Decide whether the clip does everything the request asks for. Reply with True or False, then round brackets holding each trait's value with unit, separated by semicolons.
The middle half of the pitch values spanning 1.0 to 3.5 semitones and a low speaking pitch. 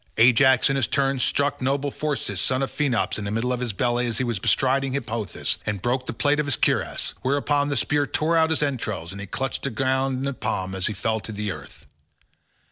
False (4.0 semitones; 130 Hz)